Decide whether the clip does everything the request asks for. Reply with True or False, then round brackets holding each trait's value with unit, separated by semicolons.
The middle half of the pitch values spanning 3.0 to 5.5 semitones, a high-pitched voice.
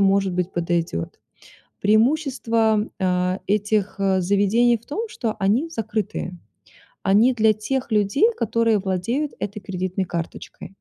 True (3.4 semitones; 205 Hz)